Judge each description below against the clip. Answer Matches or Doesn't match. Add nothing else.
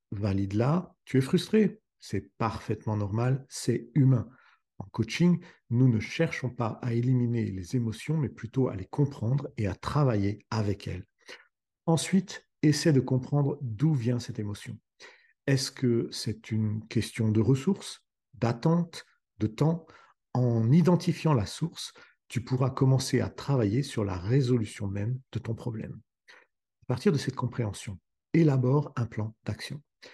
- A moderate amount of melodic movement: Matches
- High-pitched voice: Doesn't match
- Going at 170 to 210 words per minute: Doesn't match